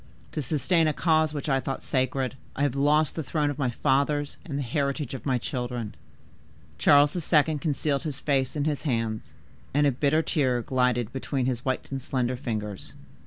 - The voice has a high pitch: No, medium, 140 Hz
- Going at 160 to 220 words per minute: Yes, average, 185 wpm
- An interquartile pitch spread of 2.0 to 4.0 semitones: Yes, average, 2.7 semitones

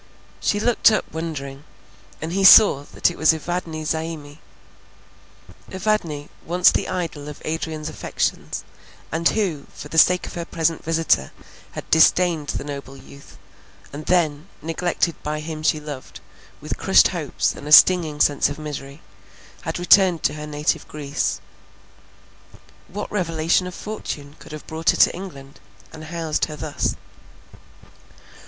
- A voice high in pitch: No, medium, 160 Hz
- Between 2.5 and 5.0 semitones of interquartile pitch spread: Yes, average, 2.8 semitones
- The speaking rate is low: No, average, 145 wpm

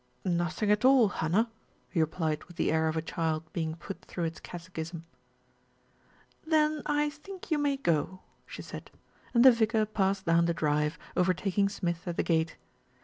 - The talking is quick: No, average, 170 wpm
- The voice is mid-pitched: Yes, medium, 180 Hz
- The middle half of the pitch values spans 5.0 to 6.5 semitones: Yes, wide, 5.5 semitones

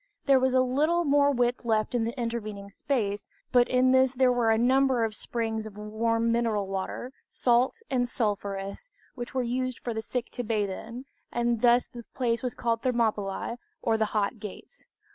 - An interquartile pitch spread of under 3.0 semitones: Yes, narrow, 2.6 semitones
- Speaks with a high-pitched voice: Yes, high, 235 Hz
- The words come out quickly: No, average, 185 wpm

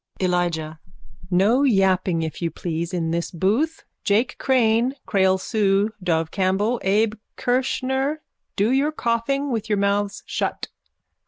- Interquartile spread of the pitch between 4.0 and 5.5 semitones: Yes, average, 5.2 semitones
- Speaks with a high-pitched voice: Yes, high, 205 Hz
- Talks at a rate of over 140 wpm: No, slow, 135 wpm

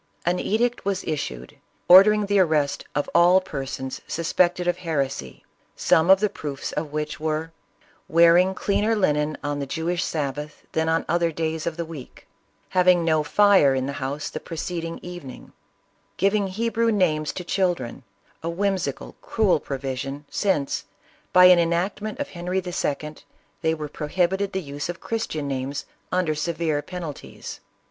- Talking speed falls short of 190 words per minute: Yes, average, 155 wpm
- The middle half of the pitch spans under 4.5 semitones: Yes, average, 3.8 semitones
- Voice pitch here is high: No, medium, 165 Hz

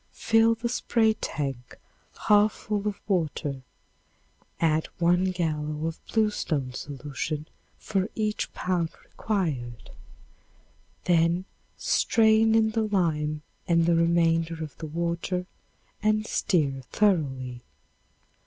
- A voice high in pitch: No, medium, 170 Hz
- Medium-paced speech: No, slow, 105 wpm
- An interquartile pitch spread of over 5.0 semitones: Yes, wide, 5.6 semitones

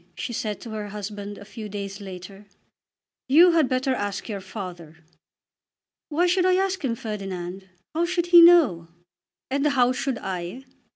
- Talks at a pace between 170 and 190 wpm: No, average, 160 wpm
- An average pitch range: No, wide, 7.2 semitones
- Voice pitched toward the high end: Yes, high, 220 Hz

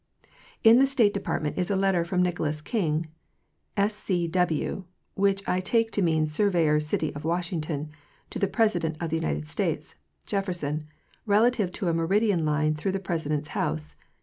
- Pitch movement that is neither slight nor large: Yes, average, 4.5 semitones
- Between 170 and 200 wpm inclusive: No, average, 160 wpm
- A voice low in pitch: No, medium, 175 Hz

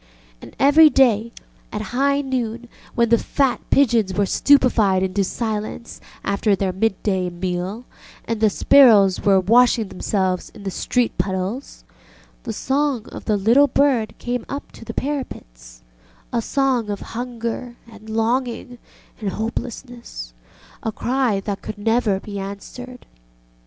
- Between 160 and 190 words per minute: No, slow, 135 wpm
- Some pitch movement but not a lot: Yes, average, 4.1 semitones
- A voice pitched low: No, high, 225 Hz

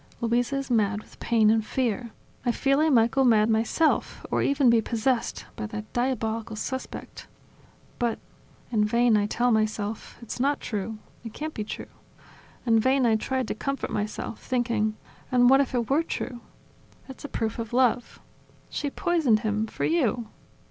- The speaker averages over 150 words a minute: Yes, average, 170 wpm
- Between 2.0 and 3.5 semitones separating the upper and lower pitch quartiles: Yes, average, 3.2 semitones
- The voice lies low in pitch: No, high, 235 Hz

